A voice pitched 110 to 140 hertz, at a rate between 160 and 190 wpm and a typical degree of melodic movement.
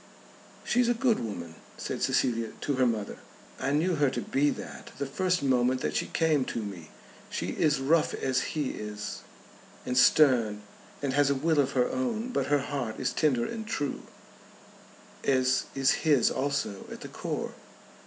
Yes: low, 135 Hz; average, 175 wpm; average, 4.0 semitones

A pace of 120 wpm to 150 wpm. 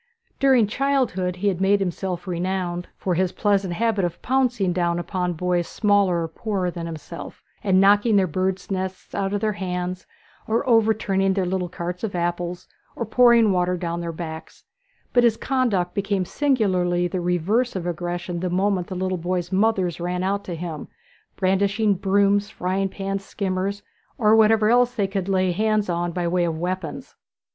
No: average, 170 wpm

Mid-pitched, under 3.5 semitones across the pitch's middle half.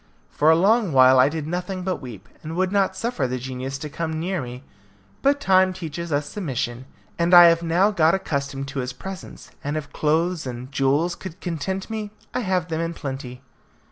No: medium, 160 Hz; wide, 5.4 semitones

